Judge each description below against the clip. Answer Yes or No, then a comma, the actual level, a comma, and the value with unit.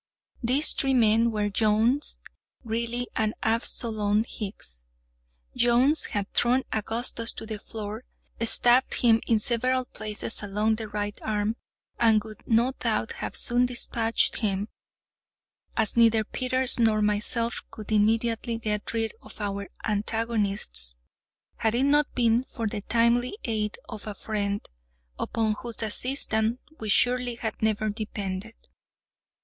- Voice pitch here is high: Yes, high, 225 Hz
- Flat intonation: Yes, narrow, 2.0 semitones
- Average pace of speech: No, slow, 130 wpm